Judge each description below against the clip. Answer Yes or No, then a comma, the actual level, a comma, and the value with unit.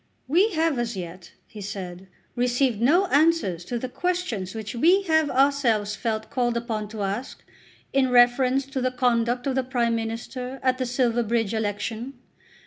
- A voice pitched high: Yes, high, 245 Hz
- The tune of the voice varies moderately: Yes, average, 3.3 semitones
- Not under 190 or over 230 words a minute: No, average, 160 wpm